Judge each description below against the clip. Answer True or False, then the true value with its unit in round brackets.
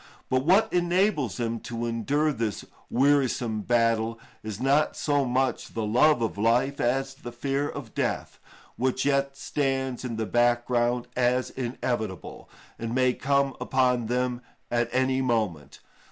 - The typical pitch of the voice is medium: False (125 Hz)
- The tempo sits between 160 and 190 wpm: False (140 wpm)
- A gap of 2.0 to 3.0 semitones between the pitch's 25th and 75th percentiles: True (2.7 semitones)